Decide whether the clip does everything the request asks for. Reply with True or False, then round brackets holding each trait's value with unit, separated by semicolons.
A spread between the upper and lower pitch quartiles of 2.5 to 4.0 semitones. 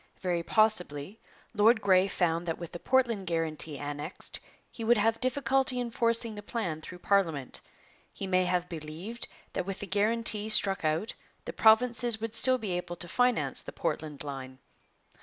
False (5.3 semitones)